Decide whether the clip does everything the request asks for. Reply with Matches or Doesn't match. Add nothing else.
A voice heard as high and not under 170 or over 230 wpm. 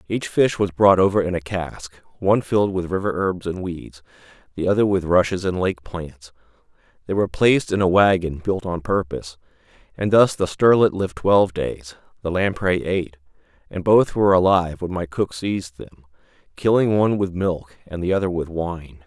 Doesn't match